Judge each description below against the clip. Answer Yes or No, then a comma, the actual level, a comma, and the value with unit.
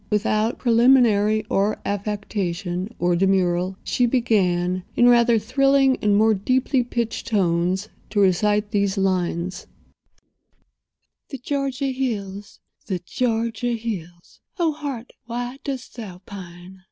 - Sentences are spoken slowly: Yes, slow, 115 wpm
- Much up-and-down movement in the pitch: No, average, 4.3 semitones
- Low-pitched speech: No, high, 210 Hz